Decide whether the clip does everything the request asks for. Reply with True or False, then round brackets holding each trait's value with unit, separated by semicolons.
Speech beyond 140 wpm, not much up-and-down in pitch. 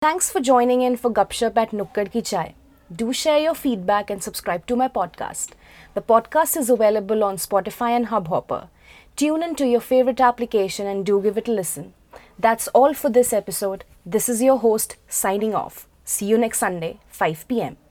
False (190 wpm; 3.7 semitones)